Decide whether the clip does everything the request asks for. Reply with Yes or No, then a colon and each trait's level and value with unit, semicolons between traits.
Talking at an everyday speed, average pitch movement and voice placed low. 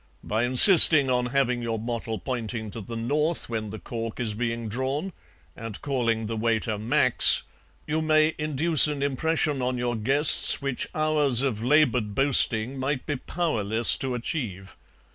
Yes: average, 155 wpm; average, 4.2 semitones; low, 125 Hz